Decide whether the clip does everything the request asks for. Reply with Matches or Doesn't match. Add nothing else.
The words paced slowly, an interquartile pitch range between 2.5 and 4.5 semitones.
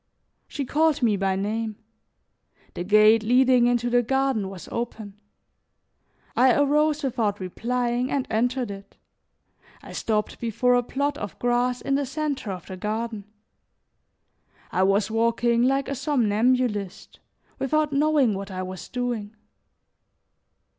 Matches